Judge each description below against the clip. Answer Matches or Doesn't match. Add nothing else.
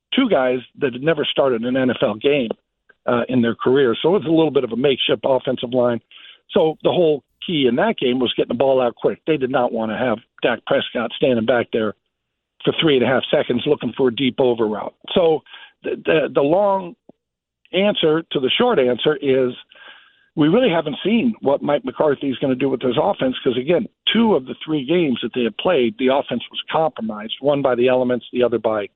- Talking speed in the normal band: Doesn't match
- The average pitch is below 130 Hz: Doesn't match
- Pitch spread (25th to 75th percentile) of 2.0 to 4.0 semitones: Doesn't match